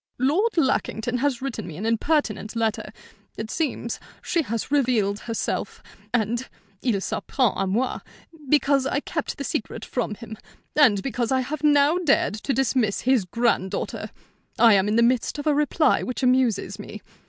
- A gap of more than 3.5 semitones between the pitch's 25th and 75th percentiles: Yes, average, 4.3 semitones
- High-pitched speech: Yes, high, 245 Hz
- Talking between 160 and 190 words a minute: Yes, average, 165 wpm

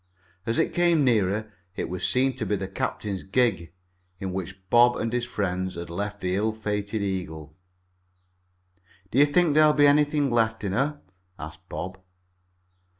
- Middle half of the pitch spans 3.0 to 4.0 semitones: No, average, 5.2 semitones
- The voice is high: No, low, 105 Hz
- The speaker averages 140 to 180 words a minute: Yes, average, 160 wpm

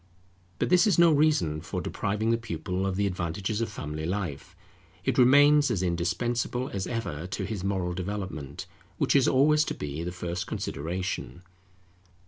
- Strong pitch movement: Yes, wide, 5.9 semitones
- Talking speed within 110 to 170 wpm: Yes, average, 160 wpm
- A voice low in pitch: Yes, low, 100 Hz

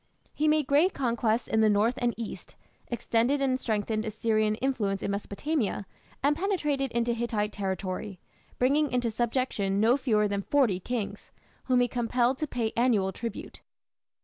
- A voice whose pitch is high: Yes, high, 235 Hz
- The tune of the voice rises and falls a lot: No, average, 3.7 semitones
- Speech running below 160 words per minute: Yes, average, 150 wpm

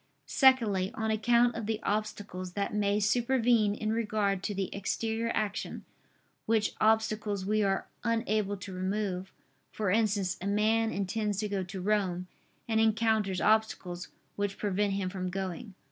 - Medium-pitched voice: No, high, 210 Hz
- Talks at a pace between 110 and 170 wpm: Yes, average, 145 wpm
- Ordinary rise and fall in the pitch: No, narrow, 2.2 semitones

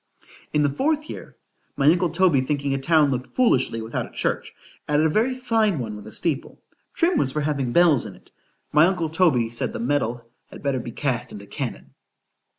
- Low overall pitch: No, medium, 145 Hz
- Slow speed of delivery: No, average, 190 wpm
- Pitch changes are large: Yes, wide, 5.7 semitones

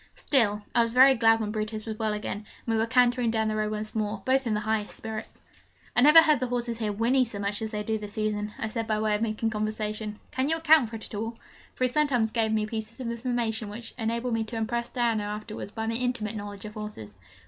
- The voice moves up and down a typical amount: No, narrow, 1.9 semitones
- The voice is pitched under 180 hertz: No, high, 220 Hz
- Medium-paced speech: No, fast, 250 wpm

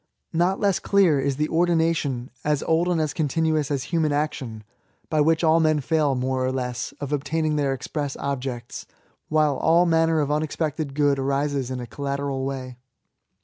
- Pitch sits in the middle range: Yes, medium, 145 Hz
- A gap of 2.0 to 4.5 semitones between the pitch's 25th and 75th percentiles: Yes, average, 3.0 semitones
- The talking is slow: No, average, 165 wpm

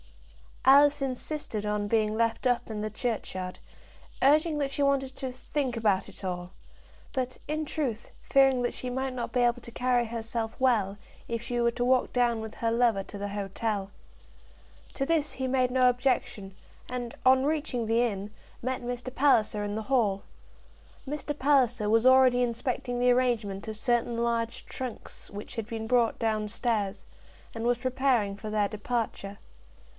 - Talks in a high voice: Yes, high, 240 Hz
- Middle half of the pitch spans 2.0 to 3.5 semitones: Yes, average, 3.1 semitones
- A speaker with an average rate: Yes, average, 170 wpm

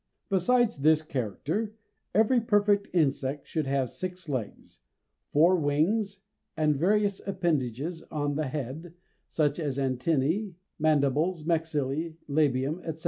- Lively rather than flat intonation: No, average, 4.7 semitones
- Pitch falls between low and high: Yes, medium, 155 Hz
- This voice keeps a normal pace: No, slow, 115 wpm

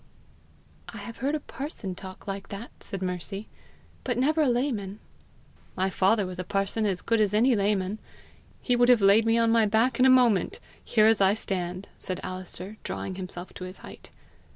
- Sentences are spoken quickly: No, average, 190 wpm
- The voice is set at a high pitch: Yes, high, 205 Hz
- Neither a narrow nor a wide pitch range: Yes, average, 3.7 semitones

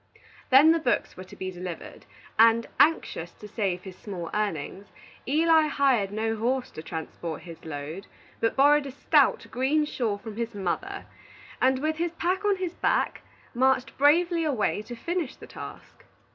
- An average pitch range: No, wide, 7.7 semitones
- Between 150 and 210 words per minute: Yes, average, 165 wpm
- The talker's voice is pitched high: Yes, high, 240 Hz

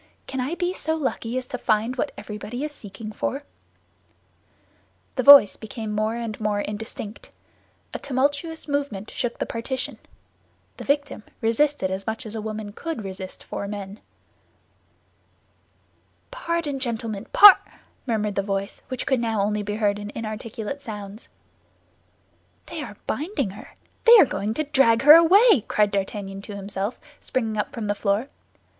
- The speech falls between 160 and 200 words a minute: No, average, 150 wpm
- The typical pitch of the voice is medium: No, high, 225 Hz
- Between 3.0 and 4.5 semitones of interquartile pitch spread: No, average, 5.2 semitones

